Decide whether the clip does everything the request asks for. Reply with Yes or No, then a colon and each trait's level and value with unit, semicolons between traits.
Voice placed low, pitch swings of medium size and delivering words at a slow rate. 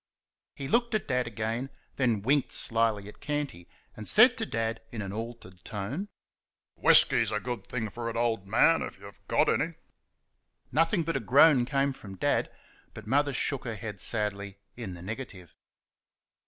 No: low, 115 Hz; average, 4.7 semitones; average, 170 wpm